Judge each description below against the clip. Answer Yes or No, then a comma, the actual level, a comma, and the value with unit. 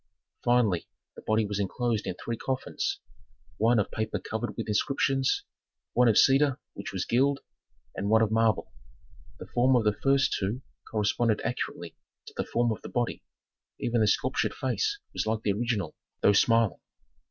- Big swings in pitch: No, average, 2.7 semitones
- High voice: No, low, 115 Hz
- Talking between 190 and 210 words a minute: No, average, 165 wpm